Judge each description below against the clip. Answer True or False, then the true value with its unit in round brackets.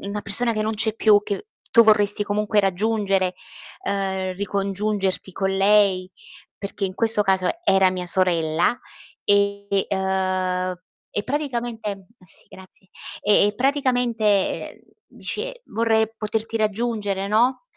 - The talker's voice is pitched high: True (205 Hz)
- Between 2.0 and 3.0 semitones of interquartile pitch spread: True (2.4 semitones)